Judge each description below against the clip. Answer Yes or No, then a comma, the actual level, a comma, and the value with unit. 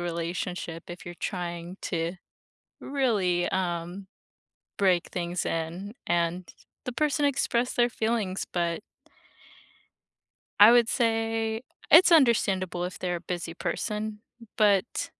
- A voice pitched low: No, medium, 185 Hz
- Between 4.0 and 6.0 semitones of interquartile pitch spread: Yes, average, 4.5 semitones